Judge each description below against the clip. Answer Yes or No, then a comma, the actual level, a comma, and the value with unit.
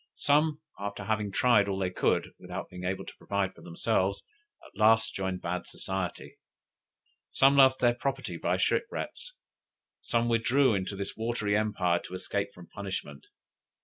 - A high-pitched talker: No, low, 100 Hz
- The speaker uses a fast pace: No, average, 150 wpm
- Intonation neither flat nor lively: Yes, average, 4.1 semitones